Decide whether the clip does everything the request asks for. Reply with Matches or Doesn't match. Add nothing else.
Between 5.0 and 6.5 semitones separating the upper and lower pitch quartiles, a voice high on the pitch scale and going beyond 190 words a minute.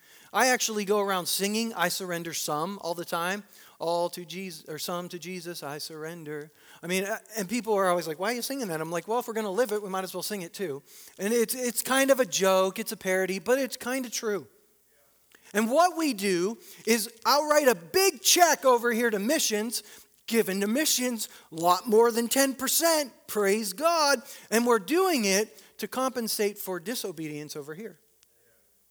Matches